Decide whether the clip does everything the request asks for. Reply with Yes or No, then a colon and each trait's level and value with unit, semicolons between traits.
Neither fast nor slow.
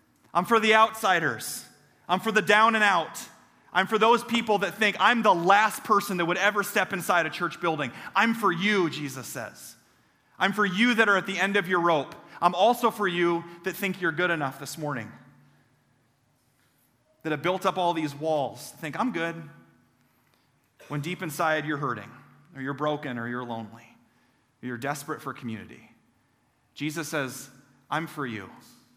Yes: average, 180 wpm